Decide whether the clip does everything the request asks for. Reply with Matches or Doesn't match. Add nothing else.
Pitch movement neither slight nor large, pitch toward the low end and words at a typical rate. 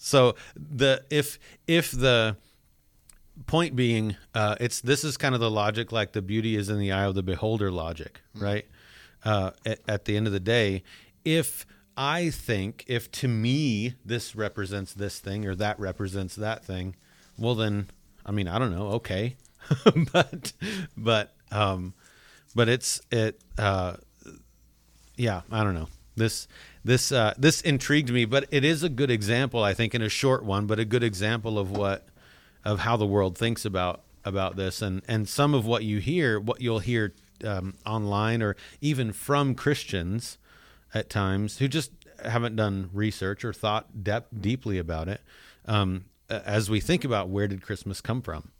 Matches